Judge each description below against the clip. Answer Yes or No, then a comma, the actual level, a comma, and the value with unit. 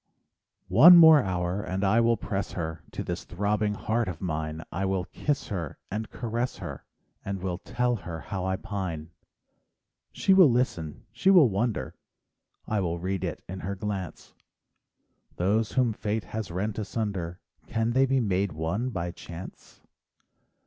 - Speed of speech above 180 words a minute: No, average, 155 wpm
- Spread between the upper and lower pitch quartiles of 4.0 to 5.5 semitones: Yes, average, 4.3 semitones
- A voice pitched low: Yes, low, 100 Hz